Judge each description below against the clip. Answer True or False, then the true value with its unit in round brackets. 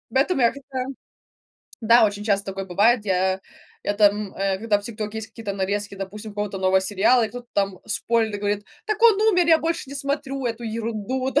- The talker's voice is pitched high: True (215 Hz)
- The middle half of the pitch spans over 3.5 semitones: True (4.1 semitones)